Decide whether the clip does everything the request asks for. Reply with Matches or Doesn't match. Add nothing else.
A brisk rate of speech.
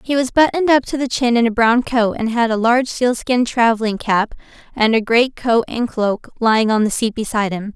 Matches